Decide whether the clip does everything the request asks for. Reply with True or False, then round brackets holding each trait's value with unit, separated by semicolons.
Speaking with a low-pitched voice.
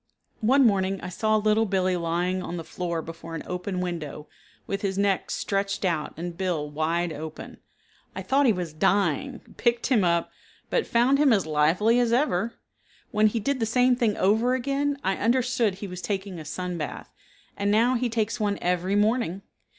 False (200 Hz)